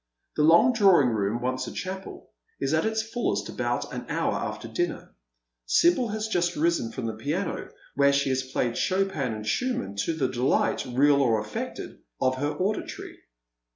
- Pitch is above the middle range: No, medium, 145 Hz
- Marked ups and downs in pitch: Yes, wide, 7.3 semitones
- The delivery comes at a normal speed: Yes, average, 170 wpm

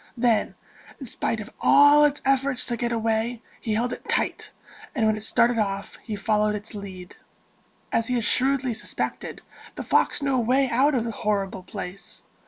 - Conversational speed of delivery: Yes, average, 185 wpm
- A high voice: Yes, high, 230 Hz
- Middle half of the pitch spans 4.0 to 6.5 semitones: No, average, 3.3 semitones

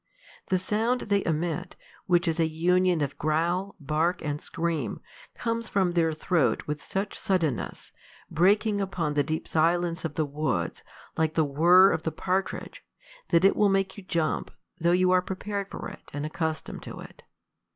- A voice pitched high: No, medium, 170 Hz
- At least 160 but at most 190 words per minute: Yes, average, 170 wpm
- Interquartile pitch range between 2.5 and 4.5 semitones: Yes, average, 3.2 semitones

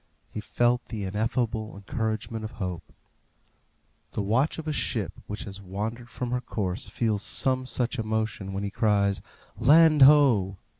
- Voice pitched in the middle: No, low, 110 Hz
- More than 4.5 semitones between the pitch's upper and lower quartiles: No, average, 3.6 semitones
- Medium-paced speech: Yes, average, 150 wpm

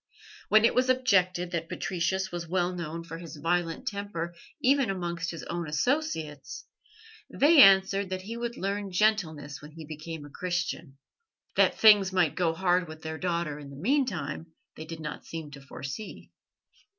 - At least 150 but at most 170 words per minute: Yes, average, 165 wpm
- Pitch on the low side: No, medium, 175 Hz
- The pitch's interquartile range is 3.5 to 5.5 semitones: Yes, average, 3.8 semitones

